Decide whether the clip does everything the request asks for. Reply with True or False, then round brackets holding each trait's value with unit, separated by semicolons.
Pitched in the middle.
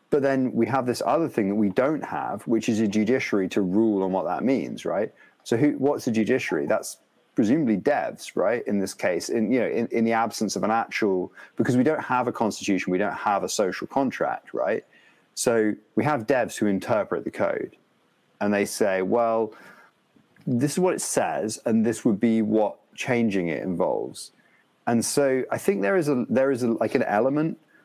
False (115 Hz)